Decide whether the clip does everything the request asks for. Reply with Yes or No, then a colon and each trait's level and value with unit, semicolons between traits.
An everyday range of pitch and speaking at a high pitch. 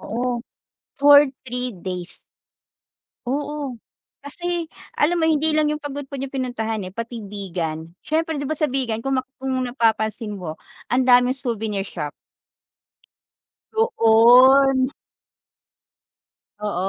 Yes: average, 4.7 semitones; very high, 250 Hz